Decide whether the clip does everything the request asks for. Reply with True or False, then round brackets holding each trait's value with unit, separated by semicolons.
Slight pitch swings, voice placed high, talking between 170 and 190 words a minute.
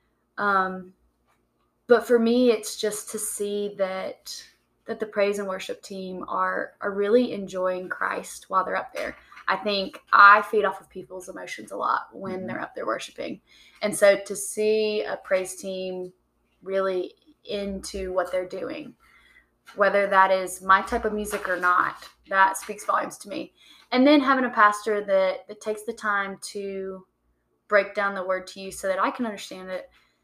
True (2.1 semitones; 200 Hz; 175 wpm)